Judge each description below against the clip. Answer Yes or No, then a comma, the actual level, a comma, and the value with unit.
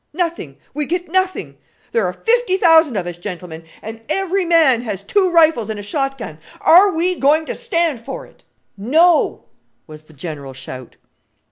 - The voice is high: Yes, very high, 275 Hz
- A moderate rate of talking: Yes, average, 170 wpm